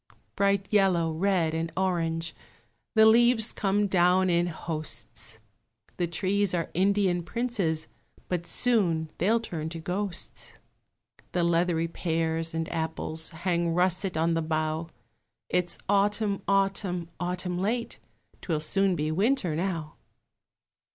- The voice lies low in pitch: No, medium, 175 Hz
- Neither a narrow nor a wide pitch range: Yes, average, 3.3 semitones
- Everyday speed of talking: No, slow, 120 wpm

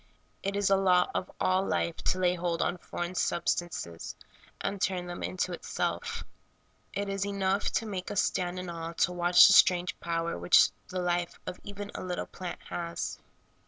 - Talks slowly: No, average, 185 wpm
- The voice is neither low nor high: Yes, medium, 180 Hz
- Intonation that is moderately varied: No, narrow, 1.9 semitones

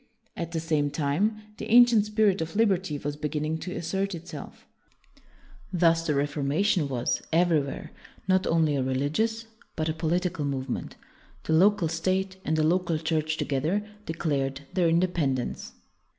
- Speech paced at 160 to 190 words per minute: No, average, 150 wpm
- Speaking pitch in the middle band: Yes, medium, 165 Hz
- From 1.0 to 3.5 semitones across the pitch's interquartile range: No, average, 4.1 semitones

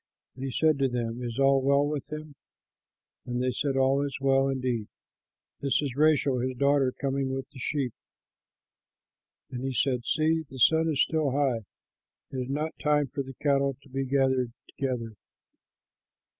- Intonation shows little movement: Yes, narrow, 1.9 semitones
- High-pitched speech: No, low, 135 Hz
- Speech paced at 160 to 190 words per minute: Yes, average, 170 wpm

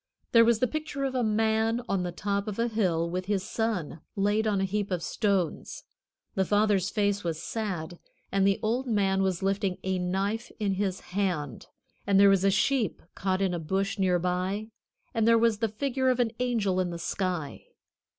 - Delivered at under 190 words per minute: No, average, 200 wpm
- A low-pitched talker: No, high, 200 Hz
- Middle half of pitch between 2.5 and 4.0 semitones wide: Yes, average, 3.1 semitones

